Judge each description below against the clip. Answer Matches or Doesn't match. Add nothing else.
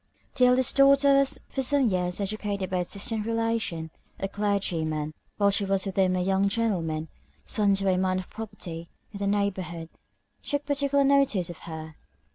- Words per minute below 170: Doesn't match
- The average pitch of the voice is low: Doesn't match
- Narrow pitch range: Doesn't match